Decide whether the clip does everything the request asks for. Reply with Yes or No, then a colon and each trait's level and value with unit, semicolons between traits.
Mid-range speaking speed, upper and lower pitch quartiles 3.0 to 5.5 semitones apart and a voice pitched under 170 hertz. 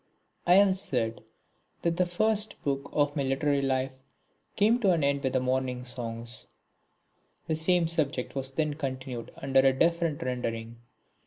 Yes: average, 155 wpm; average, 4.4 semitones; medium, 140 Hz